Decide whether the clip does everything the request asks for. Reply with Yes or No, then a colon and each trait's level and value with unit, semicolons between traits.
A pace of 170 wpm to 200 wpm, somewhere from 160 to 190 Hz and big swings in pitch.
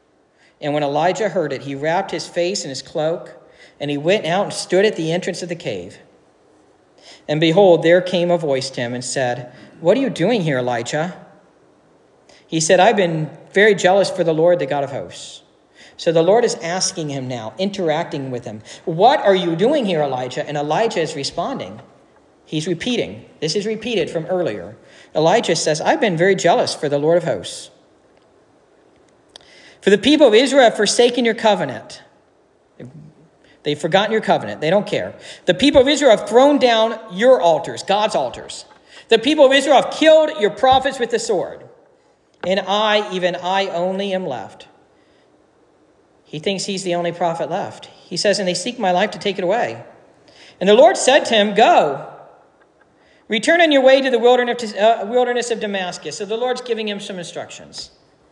Yes: average, 180 wpm; medium, 185 Hz; wide, 5.8 semitones